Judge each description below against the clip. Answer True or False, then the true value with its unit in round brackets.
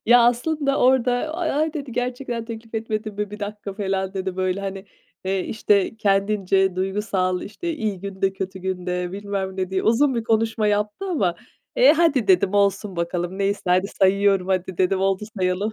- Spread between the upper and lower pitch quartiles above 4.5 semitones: False (3.1 semitones)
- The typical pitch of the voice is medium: False (200 Hz)